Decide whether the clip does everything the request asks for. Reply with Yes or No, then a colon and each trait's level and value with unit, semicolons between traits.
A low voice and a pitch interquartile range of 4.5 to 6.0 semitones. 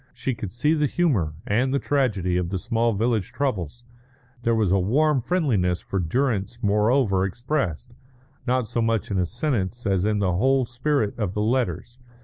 Yes: low, 115 Hz; average, 5.0 semitones